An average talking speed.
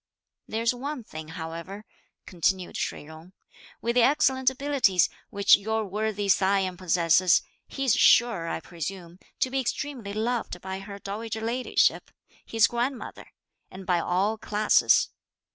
No: slow, 130 wpm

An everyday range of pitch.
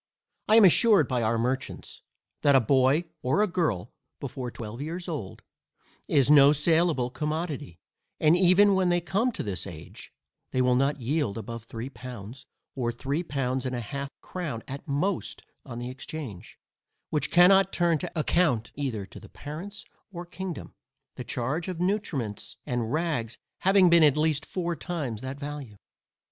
No: wide, 5.8 semitones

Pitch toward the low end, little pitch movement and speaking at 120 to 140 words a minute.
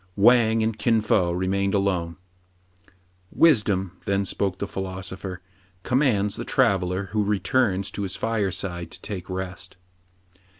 Yes: low, 100 Hz; narrow, 2.3 semitones; slow, 135 wpm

